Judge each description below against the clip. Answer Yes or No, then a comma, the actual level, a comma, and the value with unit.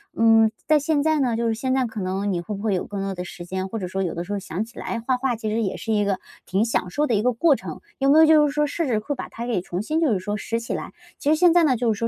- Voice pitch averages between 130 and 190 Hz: No, high, 225 Hz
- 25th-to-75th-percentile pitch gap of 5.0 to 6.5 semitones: Yes, wide, 5.5 semitones